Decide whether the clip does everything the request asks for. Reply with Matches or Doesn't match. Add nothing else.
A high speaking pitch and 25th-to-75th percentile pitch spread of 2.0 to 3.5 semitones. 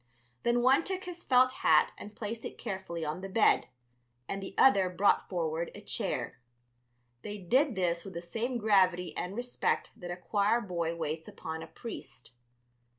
Doesn't match